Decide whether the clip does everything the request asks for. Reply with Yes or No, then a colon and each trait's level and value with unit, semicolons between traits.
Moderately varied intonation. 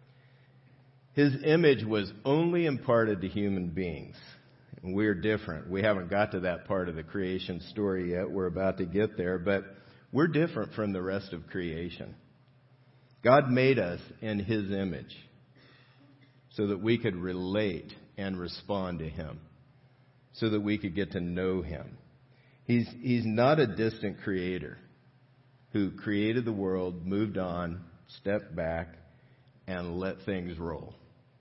No: wide, 5.8 semitones